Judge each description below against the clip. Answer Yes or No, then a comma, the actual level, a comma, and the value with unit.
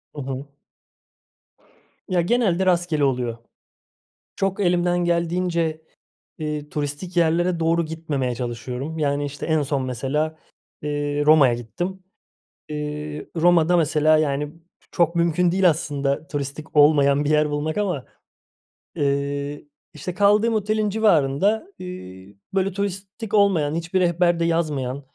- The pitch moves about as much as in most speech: Yes, average, 3.6 semitones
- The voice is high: No, medium, 155 Hz